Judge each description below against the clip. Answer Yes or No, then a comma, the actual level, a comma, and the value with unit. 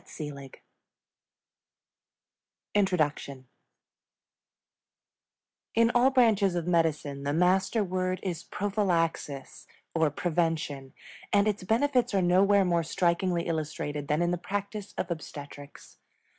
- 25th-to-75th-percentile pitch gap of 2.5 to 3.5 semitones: No, average, 4.3 semitones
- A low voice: No, medium, 175 Hz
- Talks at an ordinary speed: No, slow, 100 wpm